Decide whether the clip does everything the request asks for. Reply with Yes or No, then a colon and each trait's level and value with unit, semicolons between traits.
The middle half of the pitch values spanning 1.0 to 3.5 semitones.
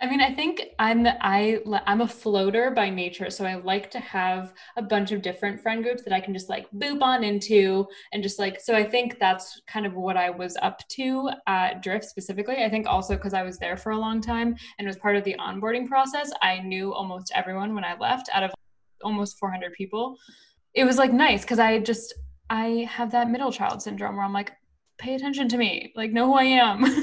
No: average, 3.9 semitones